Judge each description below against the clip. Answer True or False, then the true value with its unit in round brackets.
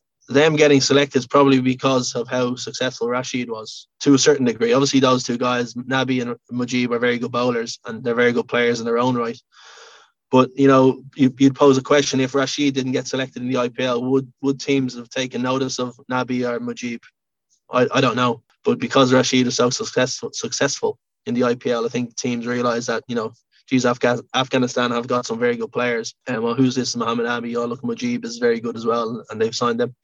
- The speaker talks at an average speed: False (220 wpm)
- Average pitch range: False (1.9 semitones)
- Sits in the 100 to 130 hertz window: True (125 Hz)